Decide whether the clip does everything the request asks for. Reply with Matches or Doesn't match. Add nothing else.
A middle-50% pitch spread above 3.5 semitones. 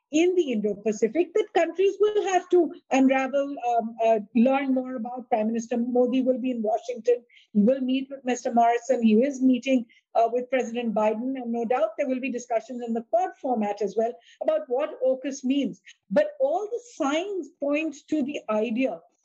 Matches